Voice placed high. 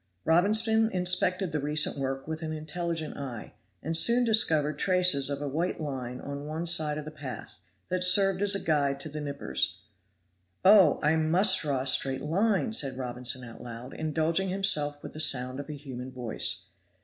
No: medium, 155 Hz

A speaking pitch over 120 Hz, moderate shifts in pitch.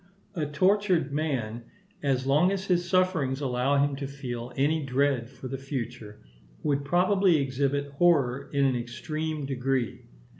Yes: medium, 140 Hz; average, 3.4 semitones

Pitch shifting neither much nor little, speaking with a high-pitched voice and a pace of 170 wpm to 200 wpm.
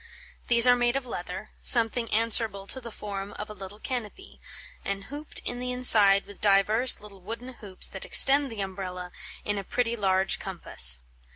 Yes: average, 3.7 semitones; high, 210 Hz; average, 175 wpm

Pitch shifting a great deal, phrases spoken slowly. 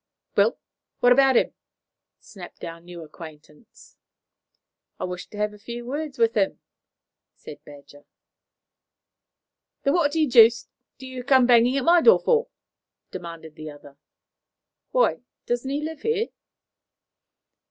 Yes: wide, 8.2 semitones; slow, 130 wpm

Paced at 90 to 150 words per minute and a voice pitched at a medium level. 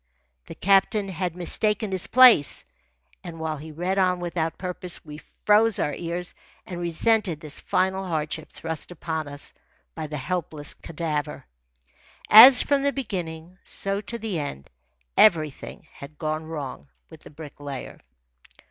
Yes: average, 140 wpm; medium, 170 Hz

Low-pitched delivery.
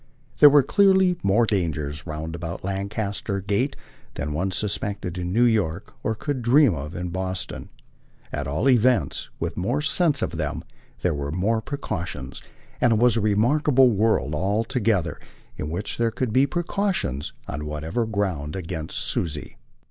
Yes: low, 100 Hz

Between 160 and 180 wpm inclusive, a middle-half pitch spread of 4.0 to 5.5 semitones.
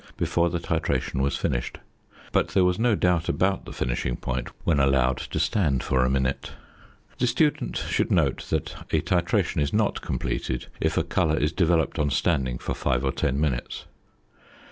Yes: average, 175 wpm; average, 5.1 semitones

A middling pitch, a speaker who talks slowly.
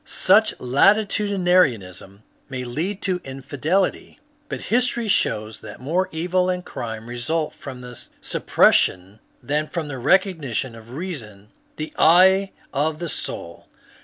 Yes: medium, 150 Hz; slow, 130 wpm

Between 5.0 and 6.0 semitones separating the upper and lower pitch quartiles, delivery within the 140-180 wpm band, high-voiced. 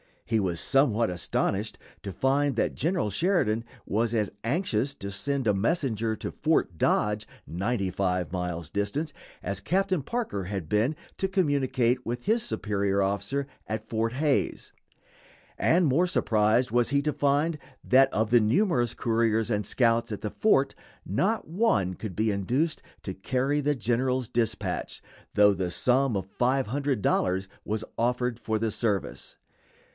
No: average, 5.3 semitones; average, 150 wpm; low, 115 Hz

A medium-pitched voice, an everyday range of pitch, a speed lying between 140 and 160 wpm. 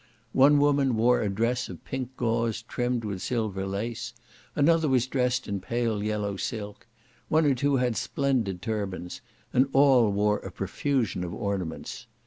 No: low, 115 Hz; average, 4.1 semitones; average, 155 wpm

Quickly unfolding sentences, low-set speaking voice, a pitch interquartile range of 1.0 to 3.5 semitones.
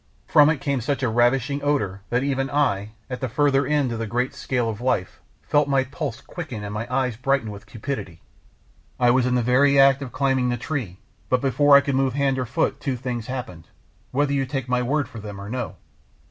Yes: fast, 220 wpm; low, 130 Hz; average, 3.0 semitones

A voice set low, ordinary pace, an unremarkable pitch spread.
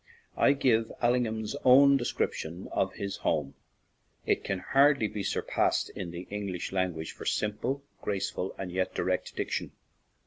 Yes: low, 105 Hz; average, 150 wpm; average, 4.9 semitones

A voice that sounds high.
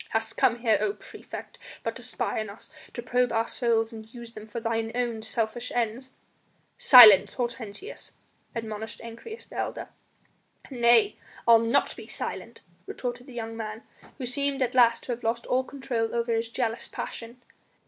Yes: high, 235 Hz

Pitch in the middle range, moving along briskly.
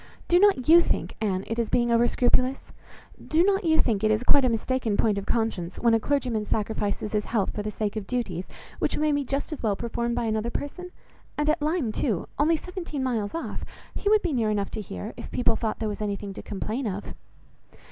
No: high, 235 Hz; fast, 225 wpm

